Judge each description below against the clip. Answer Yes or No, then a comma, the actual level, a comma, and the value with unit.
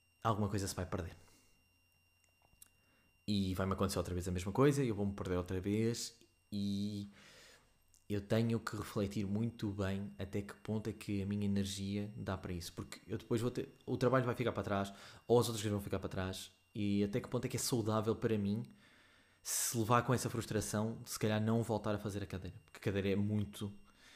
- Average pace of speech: No, fast, 210 wpm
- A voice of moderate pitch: No, low, 100 Hz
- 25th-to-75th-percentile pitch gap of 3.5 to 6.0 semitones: No, average, 2.9 semitones